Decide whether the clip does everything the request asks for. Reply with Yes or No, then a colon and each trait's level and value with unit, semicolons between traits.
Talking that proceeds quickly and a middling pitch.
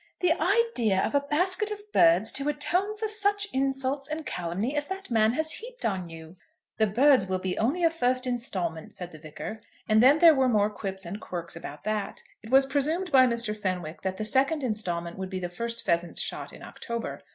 No: fast, 210 wpm; high, 235 Hz